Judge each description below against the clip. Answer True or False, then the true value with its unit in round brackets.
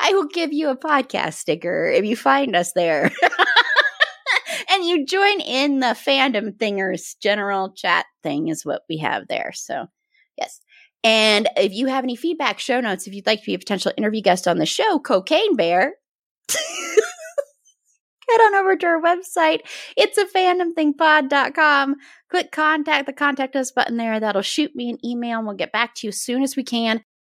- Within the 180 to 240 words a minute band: True (185 wpm)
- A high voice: True (275 Hz)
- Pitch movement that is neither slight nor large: False (7.3 semitones)